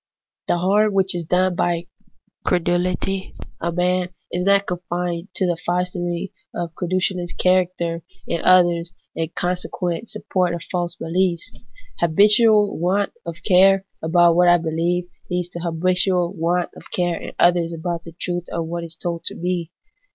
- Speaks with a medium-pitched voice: Yes, medium, 175 Hz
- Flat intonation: Yes, narrow, 1.2 semitones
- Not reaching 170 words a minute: Yes, average, 160 wpm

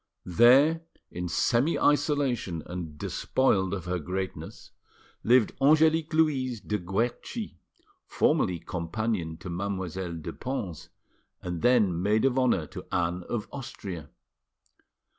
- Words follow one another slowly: Yes, slow, 115 wpm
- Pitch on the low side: Yes, low, 100 Hz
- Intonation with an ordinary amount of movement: No, wide, 6.6 semitones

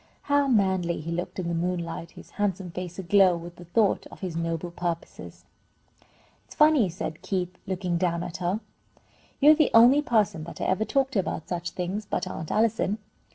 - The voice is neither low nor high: Yes, medium, 180 Hz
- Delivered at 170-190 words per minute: Yes, average, 185 wpm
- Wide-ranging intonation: No, average, 3.8 semitones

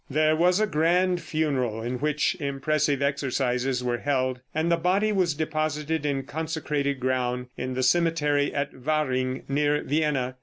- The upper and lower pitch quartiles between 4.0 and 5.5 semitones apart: No, average, 3.3 semitones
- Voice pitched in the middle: Yes, medium, 145 Hz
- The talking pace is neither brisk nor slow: Yes, average, 150 wpm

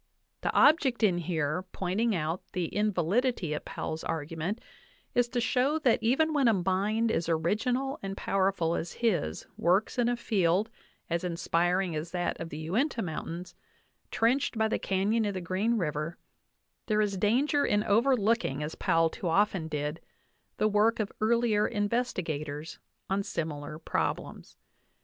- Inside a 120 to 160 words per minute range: Yes, average, 150 wpm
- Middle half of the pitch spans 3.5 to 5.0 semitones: No, wide, 5.5 semitones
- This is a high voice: Yes, high, 195 Hz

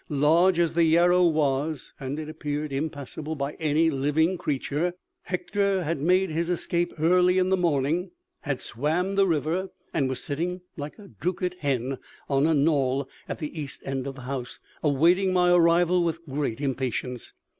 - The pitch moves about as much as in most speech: Yes, average, 4.0 semitones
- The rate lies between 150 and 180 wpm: Yes, average, 165 wpm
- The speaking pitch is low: No, medium, 160 Hz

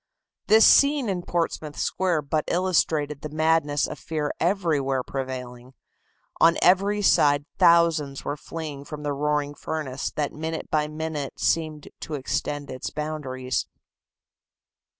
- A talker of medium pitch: Yes, medium, 150 Hz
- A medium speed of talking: No, slow, 130 wpm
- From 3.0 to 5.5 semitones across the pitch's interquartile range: No, narrow, 2.5 semitones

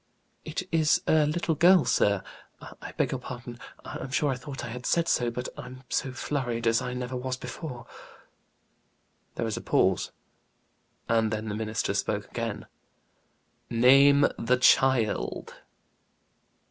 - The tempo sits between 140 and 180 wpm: Yes, average, 145 wpm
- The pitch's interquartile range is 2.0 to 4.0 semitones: Yes, average, 3.3 semitones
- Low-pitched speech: Yes, low, 125 Hz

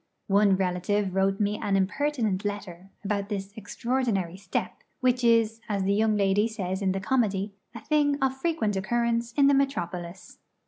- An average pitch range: Yes, average, 3.5 semitones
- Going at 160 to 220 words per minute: Yes, average, 165 wpm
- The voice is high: Yes, high, 205 Hz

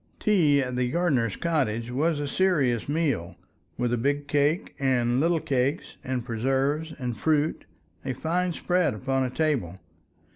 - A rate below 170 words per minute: Yes, average, 150 wpm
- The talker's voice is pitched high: No, medium, 140 Hz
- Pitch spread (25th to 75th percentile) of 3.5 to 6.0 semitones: Yes, average, 4.3 semitones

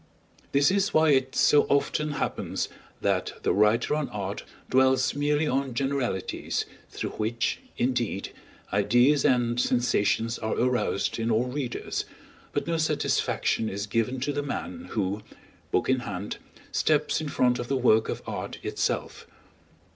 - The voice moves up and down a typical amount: Yes, average, 4.2 semitones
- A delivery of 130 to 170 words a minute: Yes, average, 145 wpm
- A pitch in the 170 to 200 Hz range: No, low, 125 Hz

